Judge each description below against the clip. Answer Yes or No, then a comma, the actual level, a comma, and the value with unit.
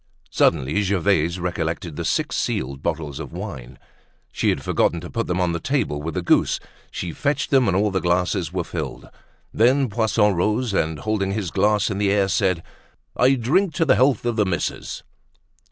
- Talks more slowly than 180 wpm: No, average, 185 wpm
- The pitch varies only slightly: No, average, 4.7 semitones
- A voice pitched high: No, very low, 95 Hz